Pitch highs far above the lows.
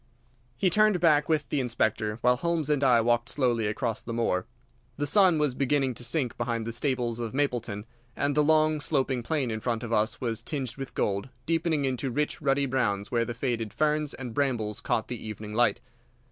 No: average, 4.0 semitones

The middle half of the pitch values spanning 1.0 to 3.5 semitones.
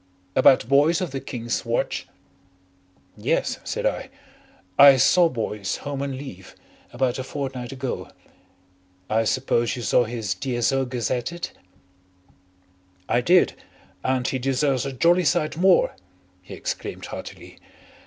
Yes: average, 2.9 semitones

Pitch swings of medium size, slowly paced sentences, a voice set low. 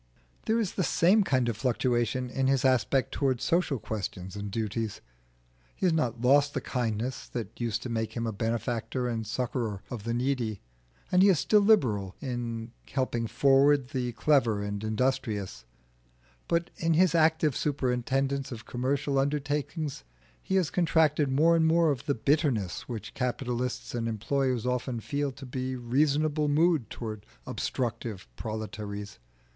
No: average, 4.2 semitones; average, 155 wpm; low, 125 Hz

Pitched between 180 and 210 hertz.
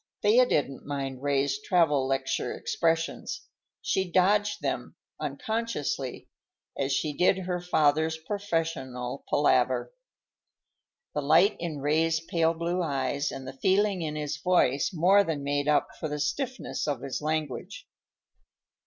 No: medium, 155 Hz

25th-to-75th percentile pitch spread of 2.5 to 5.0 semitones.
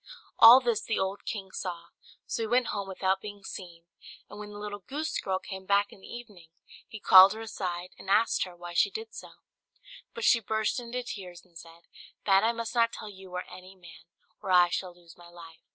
Yes: average, 3.8 semitones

